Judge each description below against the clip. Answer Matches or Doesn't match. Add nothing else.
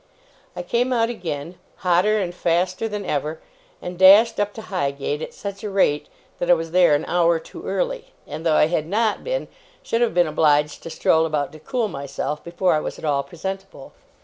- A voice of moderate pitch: Matches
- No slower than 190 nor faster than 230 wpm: Matches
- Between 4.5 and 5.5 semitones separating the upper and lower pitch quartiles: Matches